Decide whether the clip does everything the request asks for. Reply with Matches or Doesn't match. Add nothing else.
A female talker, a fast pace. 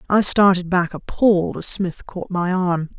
Doesn't match